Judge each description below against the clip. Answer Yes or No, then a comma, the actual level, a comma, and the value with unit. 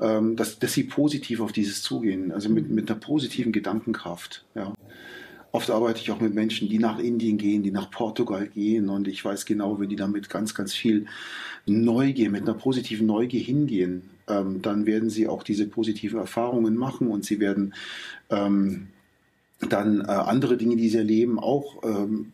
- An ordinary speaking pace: Yes, average, 175 wpm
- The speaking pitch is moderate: No, low, 110 Hz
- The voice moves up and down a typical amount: No, narrow, 2.0 semitones